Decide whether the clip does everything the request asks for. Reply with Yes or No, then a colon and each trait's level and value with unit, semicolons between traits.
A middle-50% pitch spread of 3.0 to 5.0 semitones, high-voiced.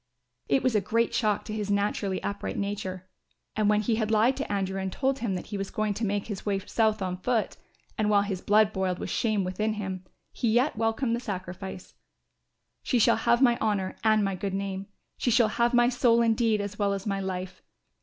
No: narrow, 2.6 semitones; high, 210 Hz